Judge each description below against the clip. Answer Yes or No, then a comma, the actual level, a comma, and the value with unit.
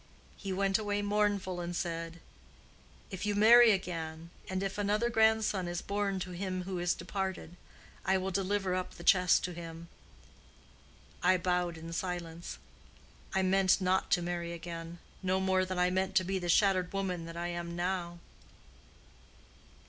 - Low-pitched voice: No, medium, 185 Hz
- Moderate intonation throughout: No, narrow, 2.0 semitones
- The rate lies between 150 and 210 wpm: Yes, average, 155 wpm